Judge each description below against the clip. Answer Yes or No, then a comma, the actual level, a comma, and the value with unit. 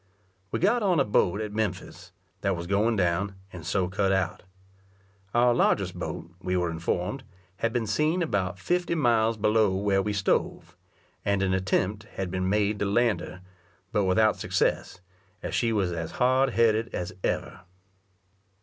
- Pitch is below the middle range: Yes, low, 100 Hz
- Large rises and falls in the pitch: No, average, 3.7 semitones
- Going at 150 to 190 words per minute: Yes, average, 165 wpm